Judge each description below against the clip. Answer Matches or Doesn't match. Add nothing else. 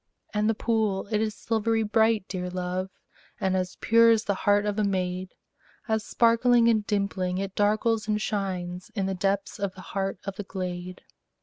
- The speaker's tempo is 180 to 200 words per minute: Matches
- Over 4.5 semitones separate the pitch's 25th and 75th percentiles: Doesn't match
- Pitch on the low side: Doesn't match